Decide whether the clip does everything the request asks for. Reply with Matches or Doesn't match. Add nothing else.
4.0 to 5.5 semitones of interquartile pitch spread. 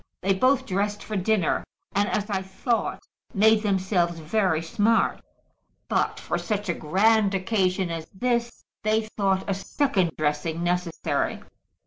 Doesn't match